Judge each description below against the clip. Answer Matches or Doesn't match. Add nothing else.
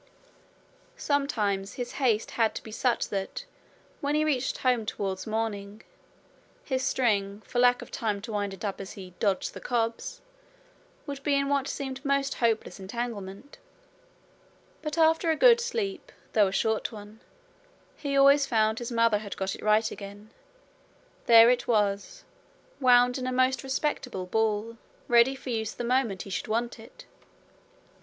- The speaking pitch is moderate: Doesn't match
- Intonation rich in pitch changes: Doesn't match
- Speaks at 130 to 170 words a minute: Matches